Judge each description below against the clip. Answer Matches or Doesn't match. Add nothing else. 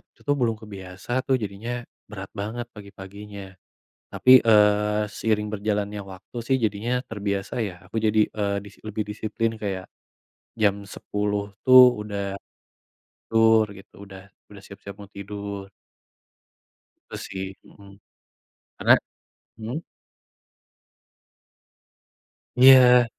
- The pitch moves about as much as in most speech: Doesn't match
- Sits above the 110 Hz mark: Doesn't match